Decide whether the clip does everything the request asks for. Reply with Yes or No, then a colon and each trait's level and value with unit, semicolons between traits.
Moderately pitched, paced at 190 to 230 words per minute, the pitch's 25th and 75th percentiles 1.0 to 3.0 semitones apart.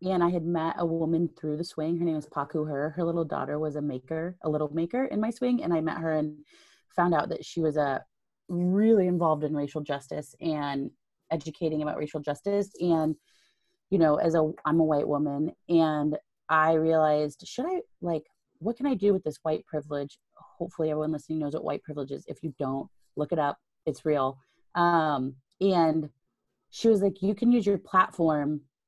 Yes: medium, 160 Hz; average, 200 wpm; average, 2.7 semitones